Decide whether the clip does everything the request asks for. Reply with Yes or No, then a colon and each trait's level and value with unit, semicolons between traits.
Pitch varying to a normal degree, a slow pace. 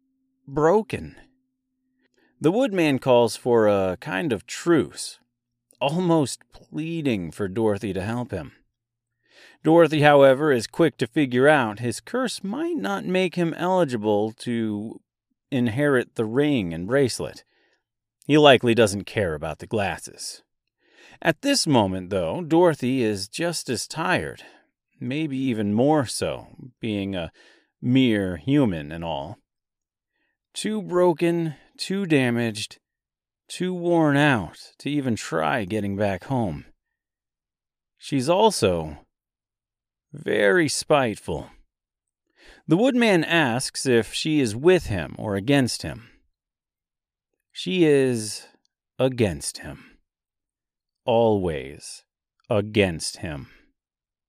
No: wide, 7.3 semitones; slow, 105 wpm